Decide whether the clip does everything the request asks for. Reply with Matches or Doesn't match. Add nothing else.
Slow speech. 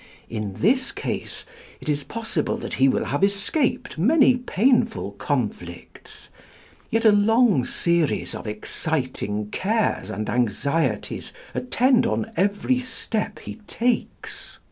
Matches